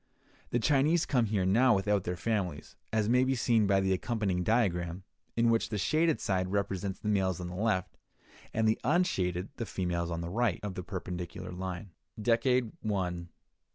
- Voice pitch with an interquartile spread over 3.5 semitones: Yes, average, 4.1 semitones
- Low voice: Yes, low, 100 Hz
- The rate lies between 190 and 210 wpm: No, average, 175 wpm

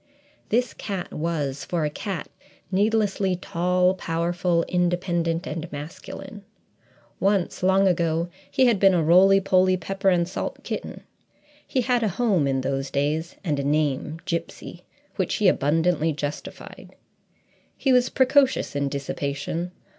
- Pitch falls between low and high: Yes, medium, 175 Hz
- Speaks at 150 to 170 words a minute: No, slow, 135 wpm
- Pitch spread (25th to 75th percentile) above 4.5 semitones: No, average, 3.8 semitones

